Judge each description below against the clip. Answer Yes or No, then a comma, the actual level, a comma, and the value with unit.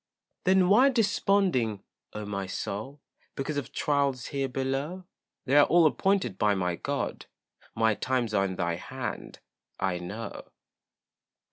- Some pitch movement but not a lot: No, wide, 7.1 semitones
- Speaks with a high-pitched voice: No, low, 130 Hz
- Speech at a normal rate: No, slow, 130 wpm